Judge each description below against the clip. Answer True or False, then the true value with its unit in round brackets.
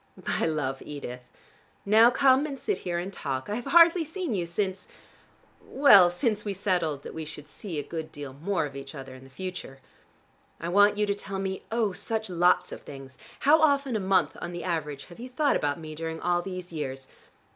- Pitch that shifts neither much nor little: False (6.1 semitones)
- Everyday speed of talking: False (210 wpm)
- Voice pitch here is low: False (180 Hz)